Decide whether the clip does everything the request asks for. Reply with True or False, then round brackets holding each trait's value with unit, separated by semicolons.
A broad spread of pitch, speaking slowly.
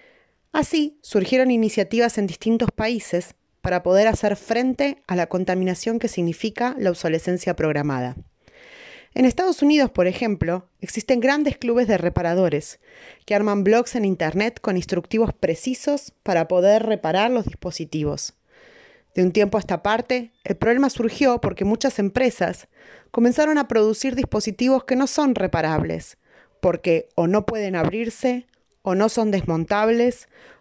False (5.8 semitones; 135 wpm)